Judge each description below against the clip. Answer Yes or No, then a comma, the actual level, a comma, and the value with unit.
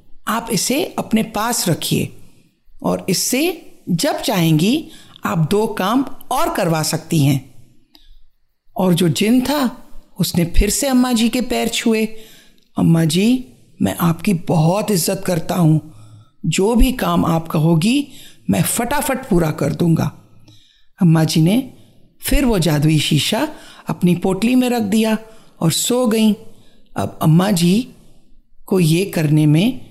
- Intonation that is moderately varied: No, wide, 6.3 semitones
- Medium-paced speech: Yes, average, 135 wpm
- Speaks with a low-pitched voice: No, high, 190 Hz